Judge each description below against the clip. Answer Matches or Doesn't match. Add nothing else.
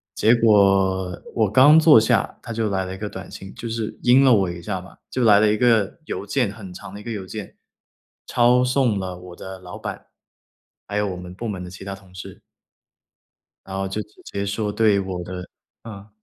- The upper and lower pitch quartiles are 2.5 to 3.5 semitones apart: Matches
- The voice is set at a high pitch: Doesn't match